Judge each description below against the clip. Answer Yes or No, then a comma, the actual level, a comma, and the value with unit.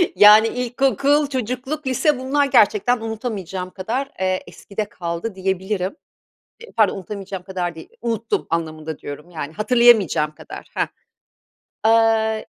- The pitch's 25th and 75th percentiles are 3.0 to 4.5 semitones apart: No, average, 5.1 semitones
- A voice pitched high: Yes, high, 215 Hz